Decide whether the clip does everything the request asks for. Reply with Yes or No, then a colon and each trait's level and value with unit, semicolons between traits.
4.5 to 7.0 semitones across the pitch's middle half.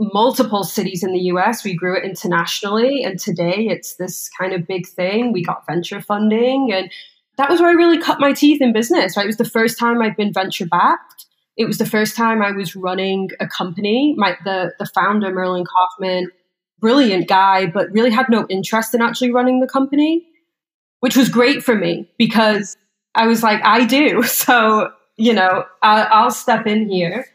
No: average, 4.1 semitones